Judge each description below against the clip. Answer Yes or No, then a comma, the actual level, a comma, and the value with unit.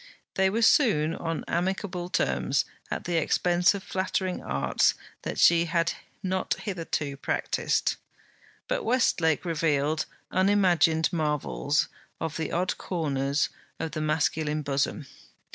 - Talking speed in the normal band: No, slow, 120 wpm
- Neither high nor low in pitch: Yes, medium, 165 Hz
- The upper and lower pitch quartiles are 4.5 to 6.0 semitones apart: No, average, 3.5 semitones